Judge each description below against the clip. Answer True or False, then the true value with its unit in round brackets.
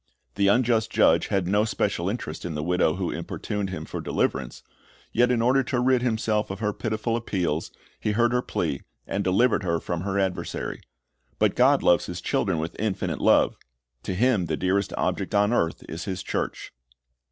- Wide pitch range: False (4.3 semitones)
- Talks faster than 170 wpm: True (185 wpm)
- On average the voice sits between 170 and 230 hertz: False (100 Hz)